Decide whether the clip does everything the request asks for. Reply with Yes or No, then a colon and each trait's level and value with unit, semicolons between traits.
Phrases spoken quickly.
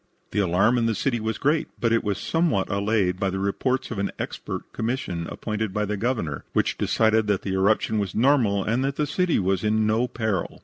Yes: fast, 215 wpm